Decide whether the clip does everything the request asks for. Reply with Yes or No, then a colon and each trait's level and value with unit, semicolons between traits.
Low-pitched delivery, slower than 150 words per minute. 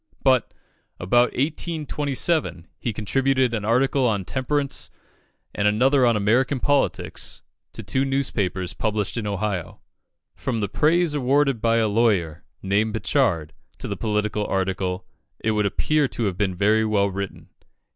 Yes: low, 110 Hz; average, 140 wpm